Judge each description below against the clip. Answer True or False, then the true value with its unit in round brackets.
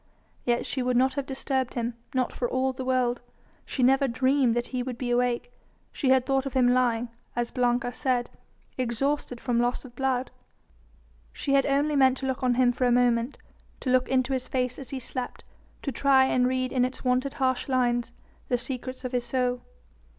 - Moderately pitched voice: False (255 Hz)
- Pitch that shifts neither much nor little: False (1.3 semitones)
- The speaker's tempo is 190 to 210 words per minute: True (200 wpm)